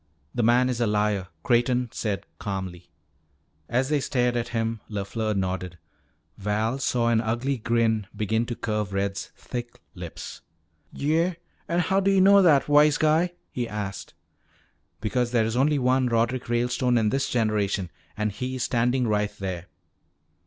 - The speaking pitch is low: Yes, low, 115 Hz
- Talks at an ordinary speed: Yes, average, 155 wpm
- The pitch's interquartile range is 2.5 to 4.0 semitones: Yes, average, 3.4 semitones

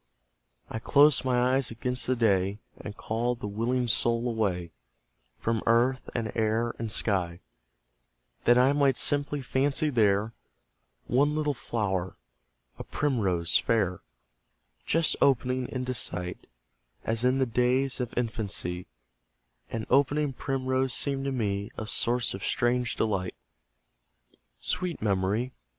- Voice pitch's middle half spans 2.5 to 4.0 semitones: Yes, average, 3.5 semitones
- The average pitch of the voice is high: No, low, 120 Hz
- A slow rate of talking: Yes, slow, 125 wpm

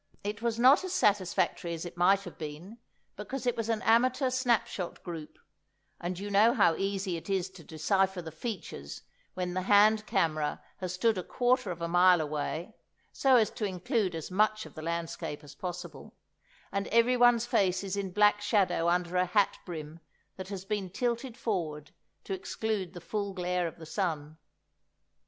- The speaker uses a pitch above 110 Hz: Yes, high, 190 Hz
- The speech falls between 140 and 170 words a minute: No, average, 180 wpm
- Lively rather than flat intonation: No, average, 3.8 semitones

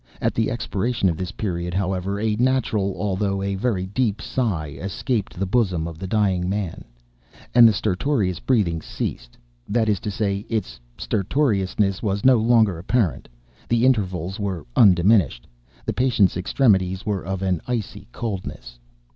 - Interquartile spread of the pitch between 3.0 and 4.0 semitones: Yes, average, 3.4 semitones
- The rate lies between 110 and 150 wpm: Yes, average, 145 wpm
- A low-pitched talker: Yes, low, 100 Hz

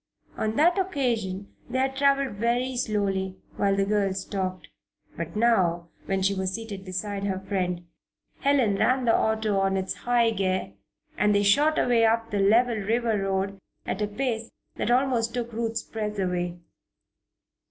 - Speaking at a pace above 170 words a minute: No, average, 165 wpm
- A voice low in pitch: No, high, 210 Hz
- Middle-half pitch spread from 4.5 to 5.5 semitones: No, average, 3.6 semitones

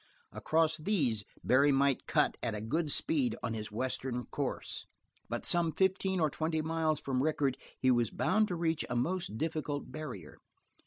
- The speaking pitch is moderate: Yes, medium, 150 Hz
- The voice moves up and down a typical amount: Yes, average, 4.5 semitones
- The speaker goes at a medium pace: Yes, average, 165 wpm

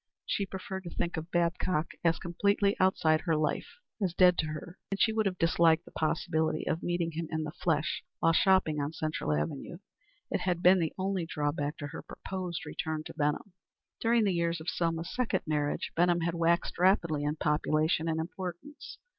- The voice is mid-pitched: Yes, medium, 170 Hz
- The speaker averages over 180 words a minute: Yes, average, 190 wpm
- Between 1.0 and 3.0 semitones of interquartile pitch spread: Yes, average, 2.7 semitones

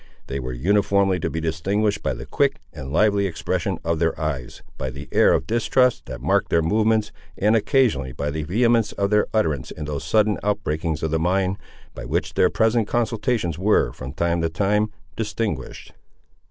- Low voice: Yes, very low, 95 Hz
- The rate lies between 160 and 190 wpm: Yes, average, 180 wpm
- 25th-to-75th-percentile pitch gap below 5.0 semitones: No, wide, 5.6 semitones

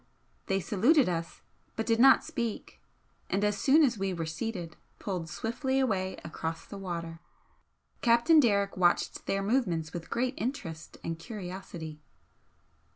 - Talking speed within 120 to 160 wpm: Yes, average, 140 wpm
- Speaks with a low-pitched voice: No, high, 195 Hz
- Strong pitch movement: Yes, wide, 5.8 semitones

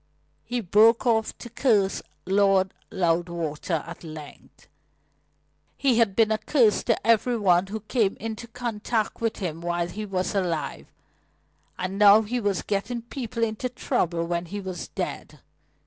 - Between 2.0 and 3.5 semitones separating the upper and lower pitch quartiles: No, average, 4.4 semitones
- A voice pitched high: Yes, high, 205 Hz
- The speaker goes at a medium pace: Yes, average, 145 wpm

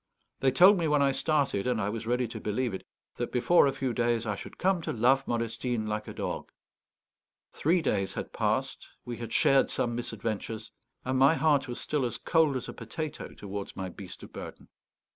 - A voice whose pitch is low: Yes, low, 120 Hz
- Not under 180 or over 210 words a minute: Yes, average, 200 wpm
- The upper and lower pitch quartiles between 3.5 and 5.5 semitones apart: Yes, average, 3.9 semitones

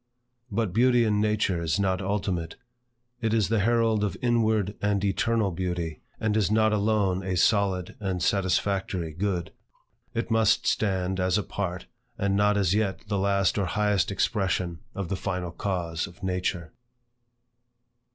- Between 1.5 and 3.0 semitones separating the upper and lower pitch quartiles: Yes, narrow, 2.6 semitones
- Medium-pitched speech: No, low, 100 Hz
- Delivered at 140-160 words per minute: Yes, average, 150 wpm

